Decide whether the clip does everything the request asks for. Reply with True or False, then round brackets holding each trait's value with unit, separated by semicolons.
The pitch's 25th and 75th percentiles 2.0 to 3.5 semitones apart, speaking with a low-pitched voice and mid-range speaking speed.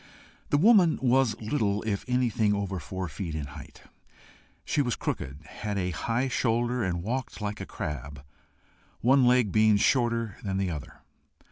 False (5.0 semitones; 110 Hz; 155 wpm)